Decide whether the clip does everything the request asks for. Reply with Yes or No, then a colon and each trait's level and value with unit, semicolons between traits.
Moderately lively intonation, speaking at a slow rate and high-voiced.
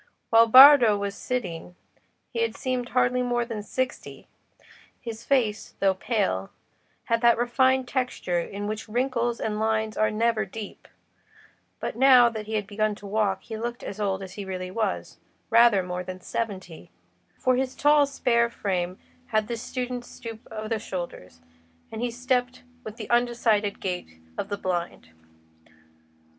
No: average, 3.4 semitones; average, 155 wpm; high, 220 Hz